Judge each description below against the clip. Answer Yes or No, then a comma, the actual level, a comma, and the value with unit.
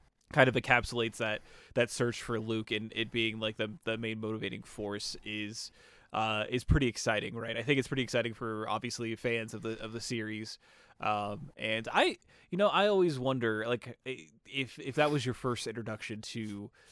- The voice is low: Yes, low, 115 Hz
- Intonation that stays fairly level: Yes, narrow, 2.2 semitones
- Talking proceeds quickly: No, average, 190 wpm